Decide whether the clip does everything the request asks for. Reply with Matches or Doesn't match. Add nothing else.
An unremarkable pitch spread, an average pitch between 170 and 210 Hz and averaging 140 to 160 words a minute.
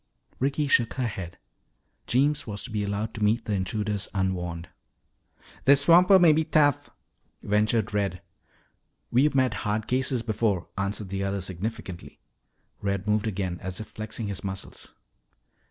Doesn't match